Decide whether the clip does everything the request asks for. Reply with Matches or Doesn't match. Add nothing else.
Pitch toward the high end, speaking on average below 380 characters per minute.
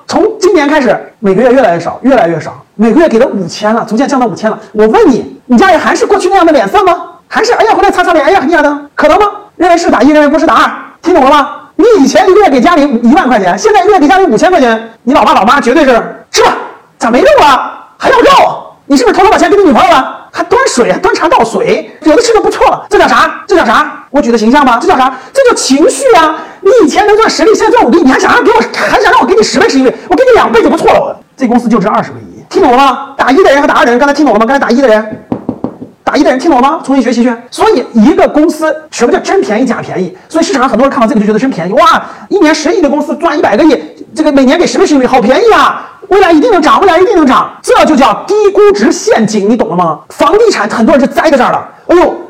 Doesn't match